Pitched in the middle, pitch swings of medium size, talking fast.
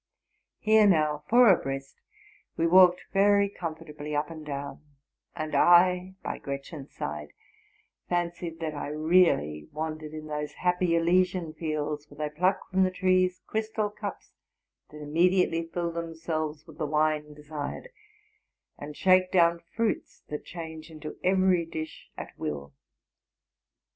No: medium, 165 Hz; average, 3.3 semitones; slow, 135 wpm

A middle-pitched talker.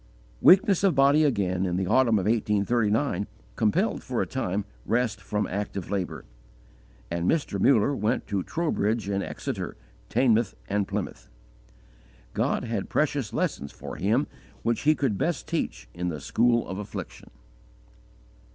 No: low, 110 Hz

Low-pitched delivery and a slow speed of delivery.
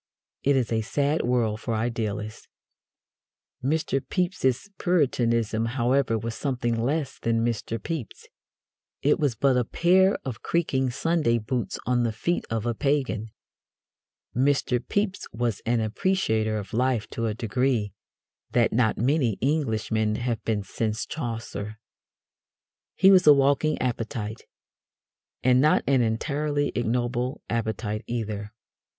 Yes: low, 120 Hz; slow, 130 wpm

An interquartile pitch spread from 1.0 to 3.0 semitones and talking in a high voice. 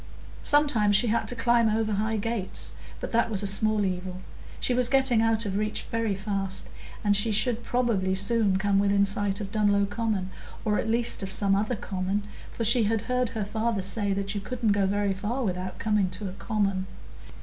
Yes: narrow, 2.6 semitones; high, 210 Hz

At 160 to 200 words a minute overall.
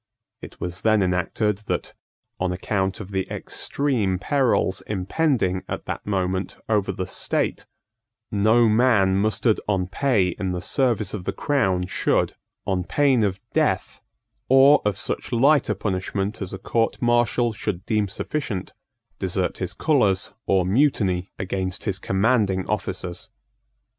No: average, 140 wpm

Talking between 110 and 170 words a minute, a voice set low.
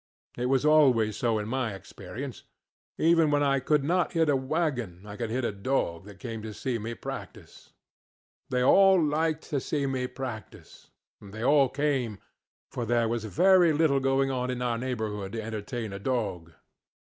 No: average, 180 wpm; low, 125 Hz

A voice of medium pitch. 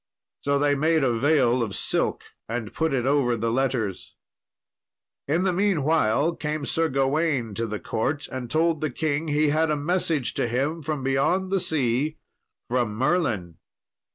Yes: medium, 145 Hz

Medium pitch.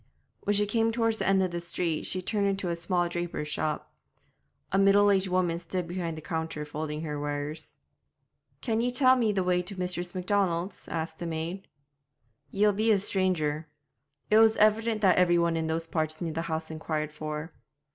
Yes: medium, 175 Hz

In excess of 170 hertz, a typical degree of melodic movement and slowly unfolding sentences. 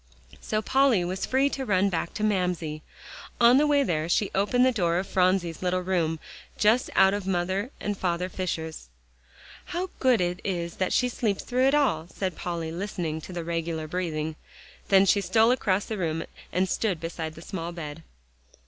No: medium, 185 Hz; average, 4.1 semitones; average, 185 wpm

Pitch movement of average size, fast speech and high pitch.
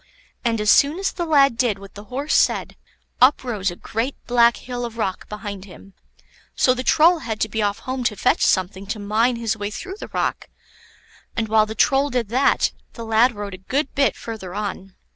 Yes: average, 3.9 semitones; fast, 210 wpm; high, 225 Hz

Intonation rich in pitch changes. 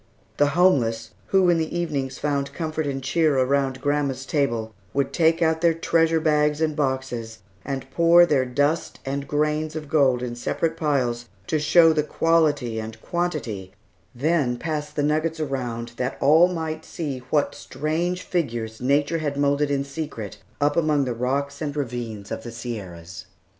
No: average, 3.9 semitones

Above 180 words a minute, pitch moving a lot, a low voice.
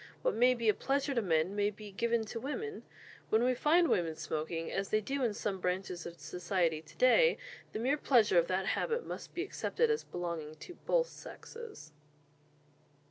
No: average, 190 wpm; wide, 7.9 semitones; high, 215 Hz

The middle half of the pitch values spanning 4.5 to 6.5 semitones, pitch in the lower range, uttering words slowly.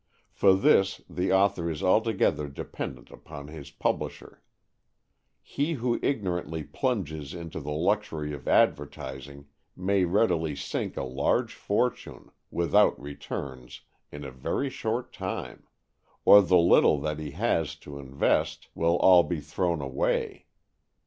Yes: average, 5.1 semitones; very low, 85 Hz; slow, 130 wpm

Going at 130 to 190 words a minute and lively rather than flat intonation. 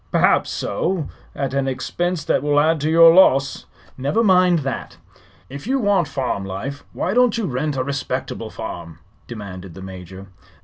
Yes: average, 165 wpm; wide, 6.2 semitones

